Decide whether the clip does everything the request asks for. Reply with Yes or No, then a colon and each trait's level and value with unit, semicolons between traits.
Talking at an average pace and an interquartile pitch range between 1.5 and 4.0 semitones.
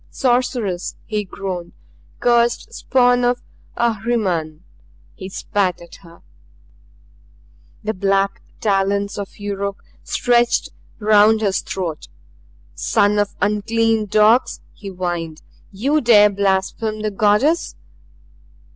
No: slow, 100 wpm; average, 2.9 semitones